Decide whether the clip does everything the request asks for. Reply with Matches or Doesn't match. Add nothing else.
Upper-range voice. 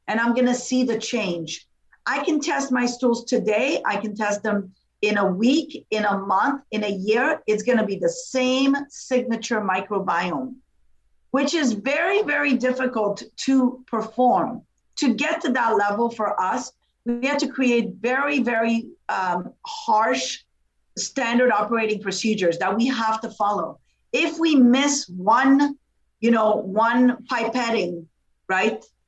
Matches